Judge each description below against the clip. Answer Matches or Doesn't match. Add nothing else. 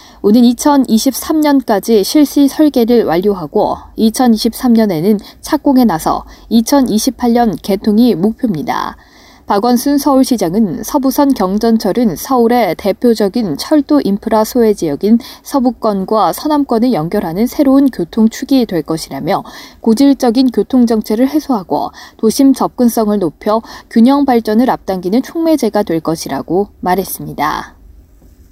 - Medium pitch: Doesn't match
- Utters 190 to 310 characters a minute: Matches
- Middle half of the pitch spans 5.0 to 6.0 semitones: Doesn't match